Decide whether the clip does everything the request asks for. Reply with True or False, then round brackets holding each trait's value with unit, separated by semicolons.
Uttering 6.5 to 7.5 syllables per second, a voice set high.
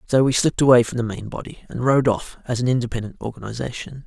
False (6.7 syllables/s; 120 Hz)